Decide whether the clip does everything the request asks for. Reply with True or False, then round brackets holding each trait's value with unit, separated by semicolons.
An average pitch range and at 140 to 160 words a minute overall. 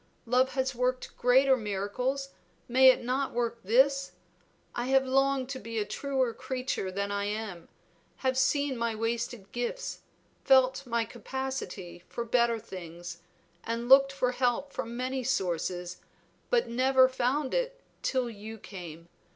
True (3.2 semitones; 145 wpm)